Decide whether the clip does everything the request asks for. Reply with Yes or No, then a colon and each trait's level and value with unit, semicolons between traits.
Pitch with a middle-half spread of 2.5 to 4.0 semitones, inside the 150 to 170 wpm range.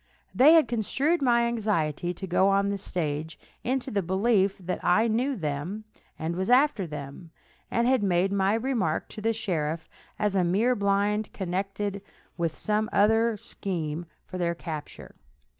No: average, 4.6 semitones; average, 160 wpm